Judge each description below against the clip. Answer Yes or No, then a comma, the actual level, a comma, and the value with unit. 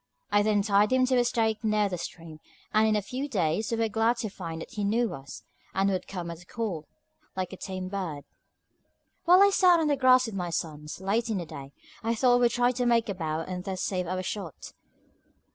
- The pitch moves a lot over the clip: No, average, 4.6 semitones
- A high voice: Yes, high, 205 Hz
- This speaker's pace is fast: Yes, fast, 235 wpm